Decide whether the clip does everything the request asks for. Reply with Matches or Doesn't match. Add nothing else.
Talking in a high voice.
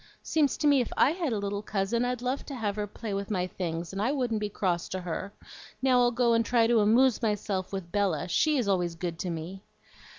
Matches